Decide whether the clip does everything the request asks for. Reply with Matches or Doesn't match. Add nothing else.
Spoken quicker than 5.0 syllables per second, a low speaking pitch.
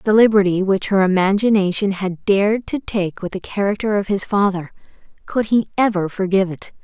Doesn't match